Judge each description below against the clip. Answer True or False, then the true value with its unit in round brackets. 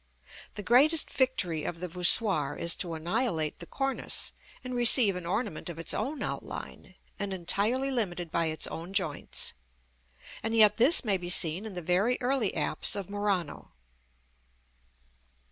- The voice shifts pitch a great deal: True (5.8 semitones)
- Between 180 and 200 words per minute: False (150 wpm)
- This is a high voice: True (195 Hz)